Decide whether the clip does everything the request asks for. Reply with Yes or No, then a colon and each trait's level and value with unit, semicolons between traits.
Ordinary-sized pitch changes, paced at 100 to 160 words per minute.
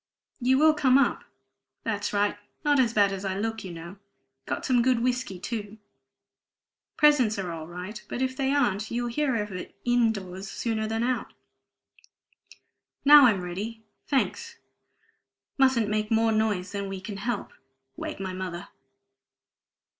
Yes: average, 4.3 semitones; average, 155 wpm